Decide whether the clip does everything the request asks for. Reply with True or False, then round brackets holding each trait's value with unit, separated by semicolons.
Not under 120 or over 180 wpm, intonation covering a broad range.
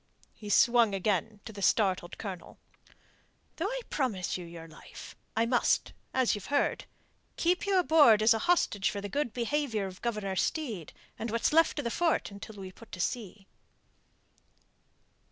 True (165 wpm; 6.2 semitones)